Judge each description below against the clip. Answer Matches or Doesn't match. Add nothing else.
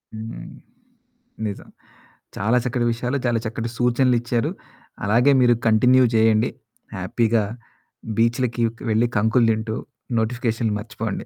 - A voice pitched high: Doesn't match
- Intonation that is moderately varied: Doesn't match